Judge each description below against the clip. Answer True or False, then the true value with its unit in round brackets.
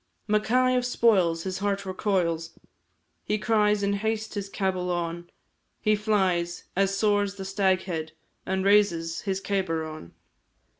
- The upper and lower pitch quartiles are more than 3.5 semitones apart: False (3.2 semitones)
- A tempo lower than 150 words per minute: True (135 wpm)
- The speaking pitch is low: False (195 Hz)